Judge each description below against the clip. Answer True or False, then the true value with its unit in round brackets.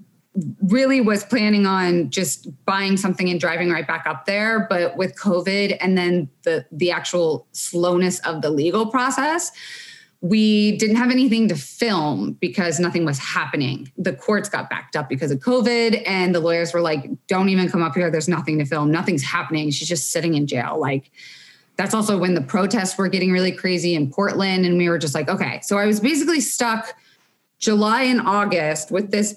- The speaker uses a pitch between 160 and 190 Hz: True (185 Hz)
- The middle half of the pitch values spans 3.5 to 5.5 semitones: True (3.9 semitones)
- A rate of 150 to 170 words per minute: False (190 wpm)